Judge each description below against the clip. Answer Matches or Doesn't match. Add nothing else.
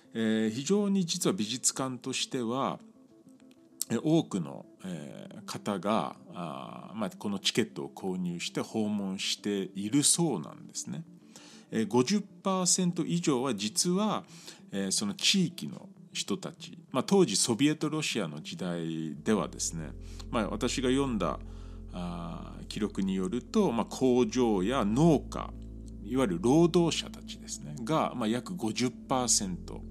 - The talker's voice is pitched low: Matches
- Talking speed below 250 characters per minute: Matches